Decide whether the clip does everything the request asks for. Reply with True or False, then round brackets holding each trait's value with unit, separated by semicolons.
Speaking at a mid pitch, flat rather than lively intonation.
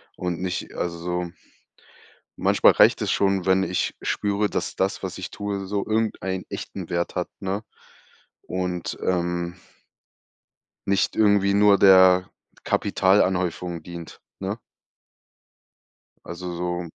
False (95 Hz; 1.9 semitones)